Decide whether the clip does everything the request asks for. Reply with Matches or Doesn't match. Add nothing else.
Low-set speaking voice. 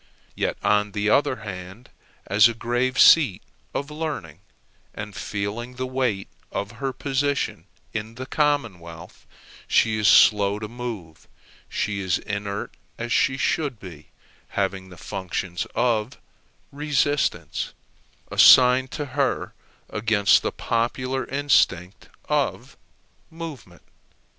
Matches